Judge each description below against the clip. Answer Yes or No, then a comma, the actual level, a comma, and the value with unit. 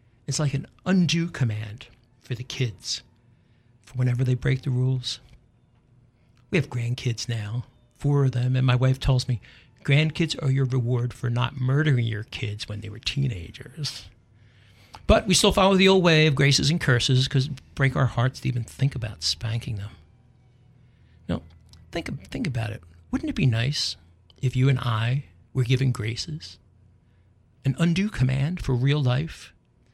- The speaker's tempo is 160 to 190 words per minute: Yes, average, 165 wpm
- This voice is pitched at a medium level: No, low, 125 Hz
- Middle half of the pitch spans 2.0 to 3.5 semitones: Yes, average, 3.1 semitones